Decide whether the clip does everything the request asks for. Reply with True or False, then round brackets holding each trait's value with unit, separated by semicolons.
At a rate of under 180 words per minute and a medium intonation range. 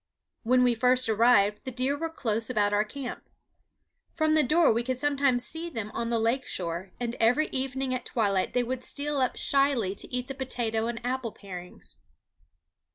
False (185 wpm; 3.2 semitones)